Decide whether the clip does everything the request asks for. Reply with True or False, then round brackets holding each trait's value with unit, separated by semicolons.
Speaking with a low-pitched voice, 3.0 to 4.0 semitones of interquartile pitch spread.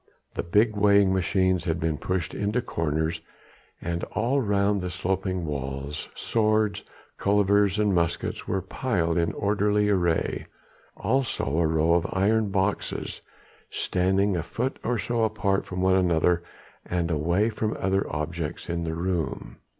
True (95 Hz; 3.5 semitones)